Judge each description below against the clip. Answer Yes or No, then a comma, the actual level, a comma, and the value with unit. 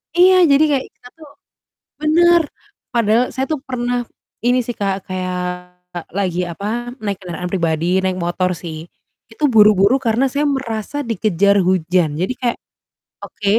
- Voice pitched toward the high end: Yes, high, 210 Hz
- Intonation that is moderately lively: No, wide, 5.7 semitones